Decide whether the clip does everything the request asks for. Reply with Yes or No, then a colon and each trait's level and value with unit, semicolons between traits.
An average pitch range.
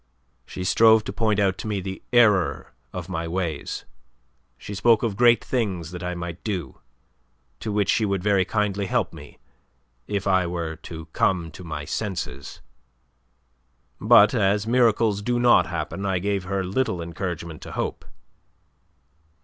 Yes: average, 3.4 semitones